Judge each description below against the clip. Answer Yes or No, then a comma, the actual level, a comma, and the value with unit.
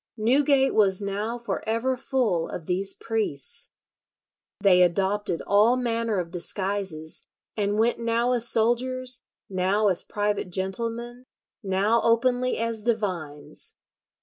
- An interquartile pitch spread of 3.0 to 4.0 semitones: Yes, average, 3.7 semitones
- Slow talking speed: Yes, slow, 120 wpm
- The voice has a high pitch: Yes, high, 215 Hz